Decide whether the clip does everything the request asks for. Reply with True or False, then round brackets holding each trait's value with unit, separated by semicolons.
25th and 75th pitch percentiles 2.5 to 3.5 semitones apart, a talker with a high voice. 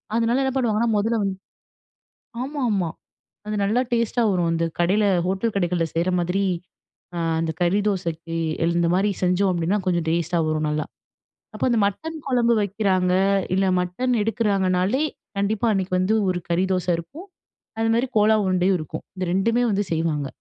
False (4.0 semitones; 195 Hz)